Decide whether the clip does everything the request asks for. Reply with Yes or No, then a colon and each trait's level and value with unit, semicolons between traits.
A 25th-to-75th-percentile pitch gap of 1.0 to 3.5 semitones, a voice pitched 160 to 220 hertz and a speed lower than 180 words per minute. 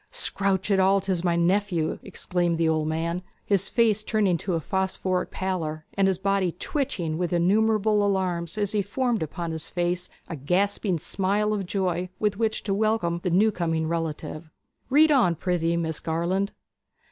Yes: average, 3.1 semitones; medium, 185 Hz; average, 170 wpm